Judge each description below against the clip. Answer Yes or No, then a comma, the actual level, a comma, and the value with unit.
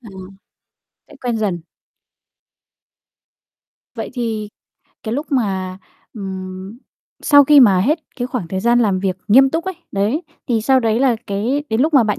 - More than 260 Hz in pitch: No, high, 225 Hz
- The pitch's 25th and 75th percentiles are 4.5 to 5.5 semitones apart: Yes, average, 5.2 semitones